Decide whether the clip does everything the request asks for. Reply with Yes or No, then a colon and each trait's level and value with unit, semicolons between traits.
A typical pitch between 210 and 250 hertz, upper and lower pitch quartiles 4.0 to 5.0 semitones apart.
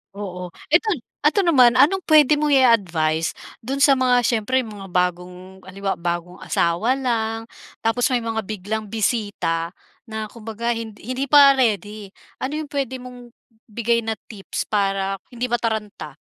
Yes: high, 225 Hz; average, 4.3 semitones